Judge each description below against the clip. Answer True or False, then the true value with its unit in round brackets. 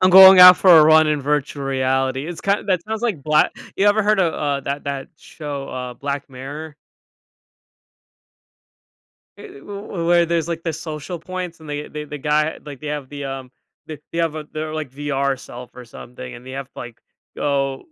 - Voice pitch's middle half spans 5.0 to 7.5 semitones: False (3.6 semitones)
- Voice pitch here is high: False (150 Hz)